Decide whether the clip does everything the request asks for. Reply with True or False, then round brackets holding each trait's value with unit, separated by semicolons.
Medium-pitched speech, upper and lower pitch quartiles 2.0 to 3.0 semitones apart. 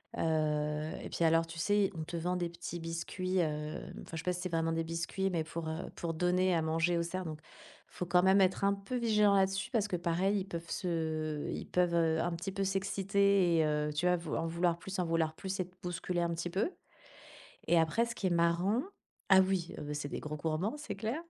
True (170 Hz; 2.7 semitones)